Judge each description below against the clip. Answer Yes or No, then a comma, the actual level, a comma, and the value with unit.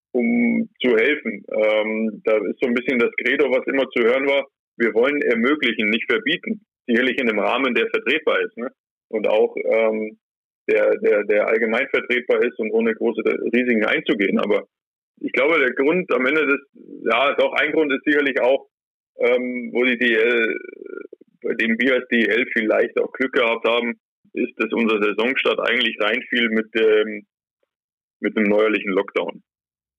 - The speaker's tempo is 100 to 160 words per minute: No, average, 170 wpm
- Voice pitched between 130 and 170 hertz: Yes, low, 135 Hz